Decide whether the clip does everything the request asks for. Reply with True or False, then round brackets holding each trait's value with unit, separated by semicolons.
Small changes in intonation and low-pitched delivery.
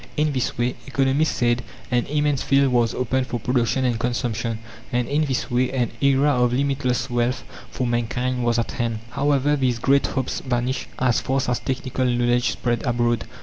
True (2.0 semitones; 125 Hz)